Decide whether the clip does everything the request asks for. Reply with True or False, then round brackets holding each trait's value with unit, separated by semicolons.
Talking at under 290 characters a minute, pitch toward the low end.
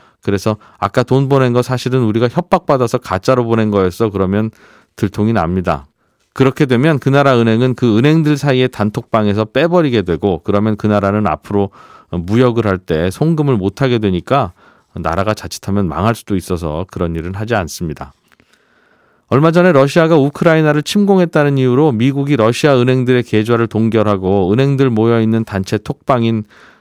False (370 characters per minute; 115 Hz)